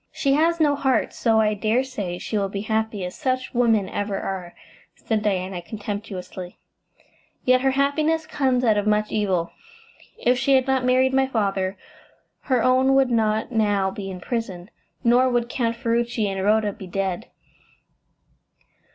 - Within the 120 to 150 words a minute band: No, average, 160 wpm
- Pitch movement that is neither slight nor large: Yes, average, 4.4 semitones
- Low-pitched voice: No, high, 220 Hz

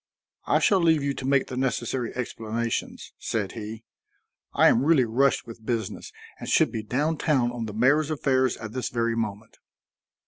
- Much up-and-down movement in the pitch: No, average, 3.4 semitones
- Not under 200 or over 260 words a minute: No, average, 175 wpm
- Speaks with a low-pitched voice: Yes, low, 120 Hz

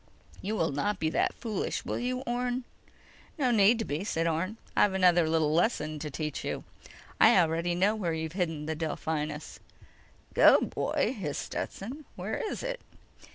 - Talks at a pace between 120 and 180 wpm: Yes, average, 165 wpm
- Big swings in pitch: Yes, wide, 5.9 semitones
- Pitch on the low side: No, medium, 175 Hz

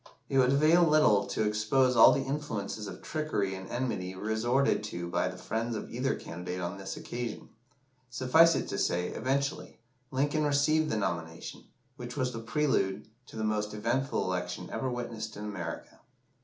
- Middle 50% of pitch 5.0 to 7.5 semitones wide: Yes, wide, 5.4 semitones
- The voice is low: Yes, low, 115 Hz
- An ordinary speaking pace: Yes, average, 170 wpm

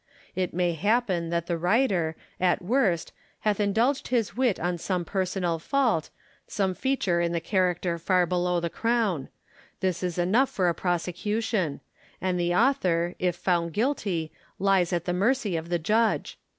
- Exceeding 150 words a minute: Yes, average, 160 wpm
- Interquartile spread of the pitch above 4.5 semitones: No, average, 3.7 semitones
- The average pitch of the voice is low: No, medium, 180 Hz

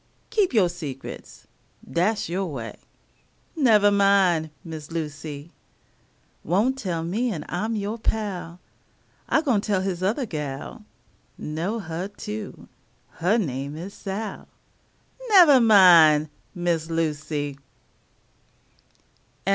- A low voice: No, medium, 180 Hz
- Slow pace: Yes, slow, 105 wpm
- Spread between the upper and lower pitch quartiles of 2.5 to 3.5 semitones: No, average, 5.2 semitones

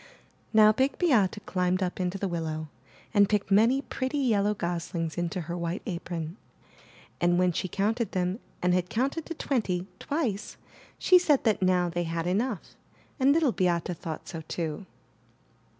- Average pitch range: Yes, average, 4.6 semitones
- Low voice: No, medium, 185 Hz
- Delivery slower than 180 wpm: Yes, average, 160 wpm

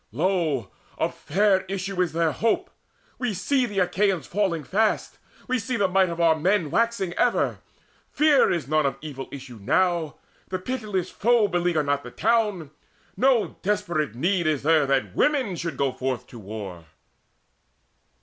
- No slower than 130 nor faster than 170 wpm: Yes, average, 160 wpm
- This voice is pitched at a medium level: Yes, medium, 180 Hz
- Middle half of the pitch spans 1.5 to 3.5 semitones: No, wide, 5.6 semitones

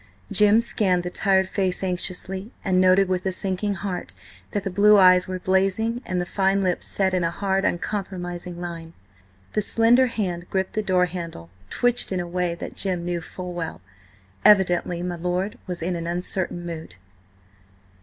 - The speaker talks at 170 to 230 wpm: Yes, average, 175 wpm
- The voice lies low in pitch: No, medium, 185 Hz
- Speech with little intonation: Yes, narrow, 1.8 semitones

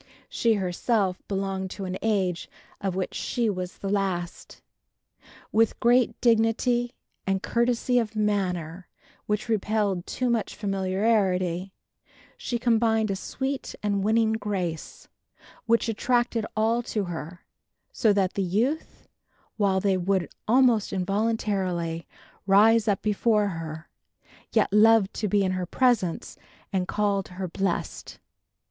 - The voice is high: Yes, high, 205 Hz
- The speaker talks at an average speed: No, slow, 125 wpm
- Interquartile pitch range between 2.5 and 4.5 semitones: Yes, average, 3.3 semitones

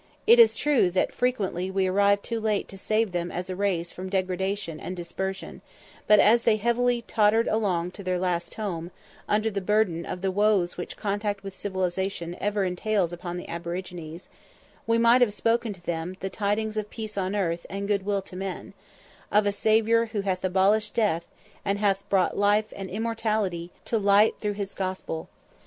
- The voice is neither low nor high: No, high, 200 Hz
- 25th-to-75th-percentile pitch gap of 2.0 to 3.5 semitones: Yes, average, 2.7 semitones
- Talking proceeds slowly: No, average, 185 wpm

